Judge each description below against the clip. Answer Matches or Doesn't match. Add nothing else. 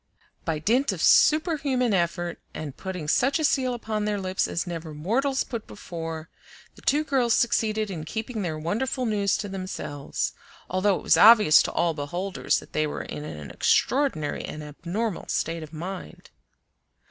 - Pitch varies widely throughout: Matches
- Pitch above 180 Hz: Matches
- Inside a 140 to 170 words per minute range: Matches